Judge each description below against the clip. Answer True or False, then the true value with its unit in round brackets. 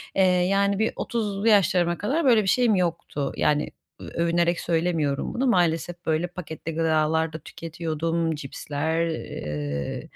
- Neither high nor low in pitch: True (170 Hz)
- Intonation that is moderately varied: True (3.1 semitones)